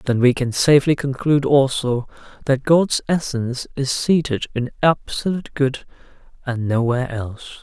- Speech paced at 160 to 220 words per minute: No, slow, 135 wpm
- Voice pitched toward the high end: No, low, 135 Hz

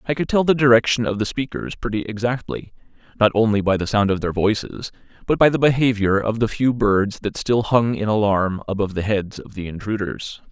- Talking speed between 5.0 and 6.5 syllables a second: Yes, 5.5 syllables/s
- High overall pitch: No, low, 110 Hz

